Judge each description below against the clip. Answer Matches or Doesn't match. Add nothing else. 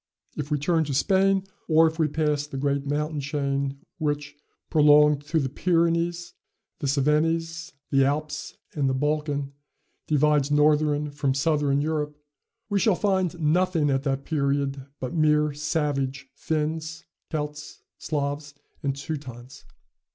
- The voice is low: Doesn't match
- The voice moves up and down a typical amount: Doesn't match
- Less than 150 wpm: Matches